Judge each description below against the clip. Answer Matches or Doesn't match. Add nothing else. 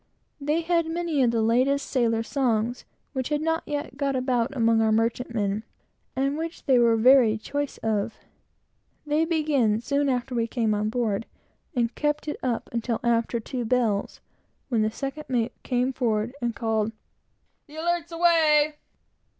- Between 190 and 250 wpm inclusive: Doesn't match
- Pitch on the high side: Matches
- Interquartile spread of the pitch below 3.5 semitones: Doesn't match